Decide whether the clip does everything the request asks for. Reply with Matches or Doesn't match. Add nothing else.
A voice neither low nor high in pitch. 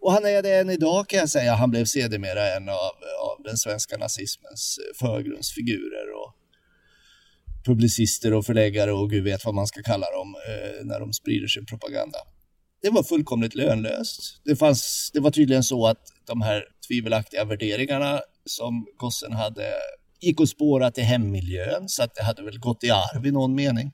Doesn't match